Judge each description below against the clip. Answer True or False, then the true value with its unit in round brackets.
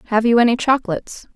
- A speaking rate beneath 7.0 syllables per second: False (7.3 syllables/s)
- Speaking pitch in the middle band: False (235 Hz)